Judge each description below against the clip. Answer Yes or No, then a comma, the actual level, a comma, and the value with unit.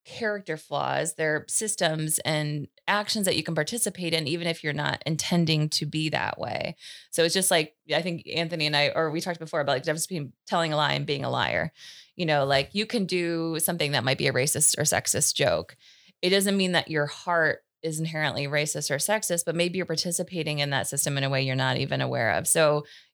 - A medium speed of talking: No, fast, 225 wpm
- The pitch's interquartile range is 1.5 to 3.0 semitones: Yes, average, 2.7 semitones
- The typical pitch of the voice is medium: Yes, medium, 160 Hz